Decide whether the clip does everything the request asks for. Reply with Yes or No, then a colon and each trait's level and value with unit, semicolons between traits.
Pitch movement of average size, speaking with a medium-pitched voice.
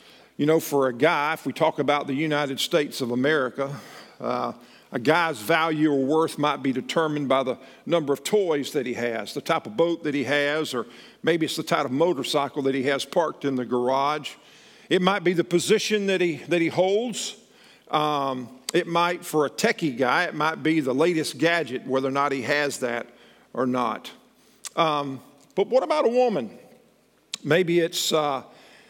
Yes: average, 3.9 semitones; medium, 155 Hz